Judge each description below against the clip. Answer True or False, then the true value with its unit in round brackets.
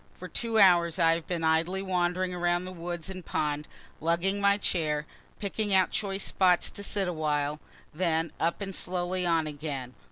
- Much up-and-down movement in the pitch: False (2.7 semitones)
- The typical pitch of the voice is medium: True (175 Hz)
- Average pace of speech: True (170 wpm)